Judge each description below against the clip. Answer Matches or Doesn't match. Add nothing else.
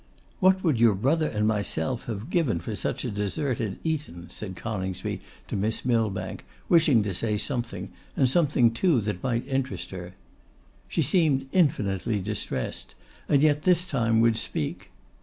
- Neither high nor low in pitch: Doesn't match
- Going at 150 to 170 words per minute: Matches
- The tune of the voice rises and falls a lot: Matches